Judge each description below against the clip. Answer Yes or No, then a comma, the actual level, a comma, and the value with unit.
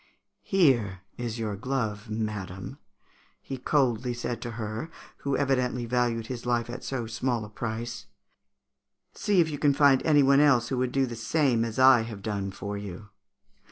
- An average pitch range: Yes, average, 3.4 semitones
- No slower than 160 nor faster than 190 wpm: Yes, average, 170 wpm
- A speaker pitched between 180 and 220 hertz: No, low, 120 Hz